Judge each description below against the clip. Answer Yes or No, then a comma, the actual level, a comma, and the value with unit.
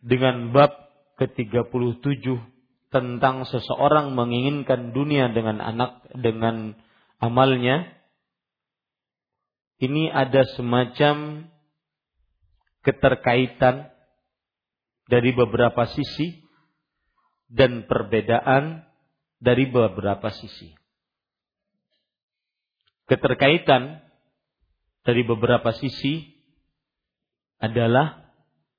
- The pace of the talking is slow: Yes, slow, 60 wpm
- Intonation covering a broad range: No, average, 3.1 semitones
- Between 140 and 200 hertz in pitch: No, low, 125 Hz